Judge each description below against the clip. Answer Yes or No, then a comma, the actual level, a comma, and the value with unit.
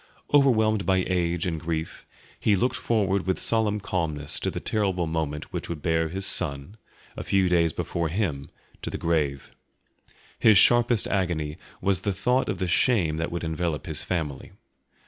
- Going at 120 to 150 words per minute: No, average, 165 wpm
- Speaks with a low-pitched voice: Yes, very low, 90 Hz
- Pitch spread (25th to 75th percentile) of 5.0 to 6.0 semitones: No, average, 3.8 semitones